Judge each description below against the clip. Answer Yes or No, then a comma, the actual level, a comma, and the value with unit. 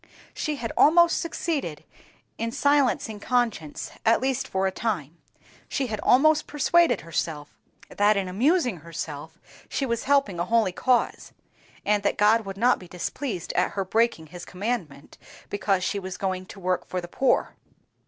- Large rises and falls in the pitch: Yes, wide, 5.8 semitones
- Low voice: No, high, 210 Hz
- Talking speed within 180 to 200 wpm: No, average, 160 wpm